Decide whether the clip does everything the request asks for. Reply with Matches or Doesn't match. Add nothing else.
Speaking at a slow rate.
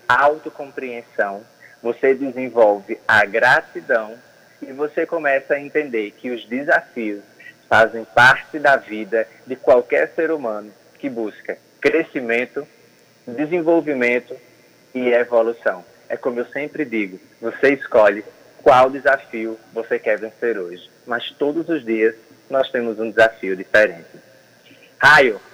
Matches